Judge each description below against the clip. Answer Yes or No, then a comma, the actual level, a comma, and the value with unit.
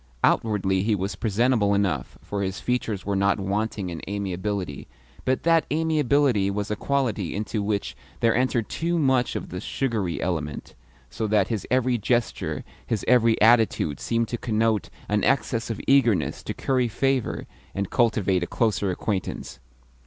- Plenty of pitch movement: No, average, 3.8 semitones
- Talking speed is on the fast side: No, average, 155 wpm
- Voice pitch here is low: Yes, low, 110 Hz